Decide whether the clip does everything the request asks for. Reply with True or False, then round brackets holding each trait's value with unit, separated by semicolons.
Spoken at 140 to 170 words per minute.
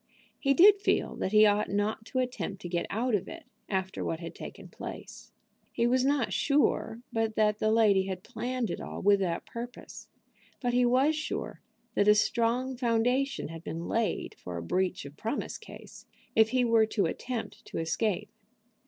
False (185 wpm)